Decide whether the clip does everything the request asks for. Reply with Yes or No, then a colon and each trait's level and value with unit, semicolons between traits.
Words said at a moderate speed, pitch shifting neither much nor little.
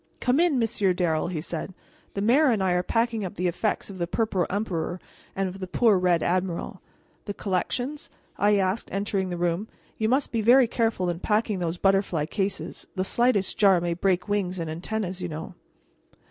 Yes: average, 190 wpm; average, 3.6 semitones